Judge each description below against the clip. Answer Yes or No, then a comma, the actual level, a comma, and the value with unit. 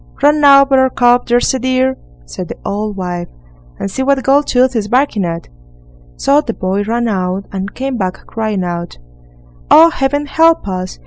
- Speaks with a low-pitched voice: No, high, 240 Hz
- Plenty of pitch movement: Yes, wide, 5.9 semitones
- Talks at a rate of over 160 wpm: Yes, average, 170 wpm